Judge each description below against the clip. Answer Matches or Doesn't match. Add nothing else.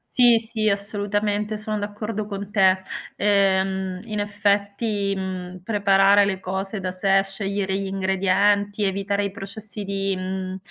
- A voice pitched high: Matches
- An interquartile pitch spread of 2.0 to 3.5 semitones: Doesn't match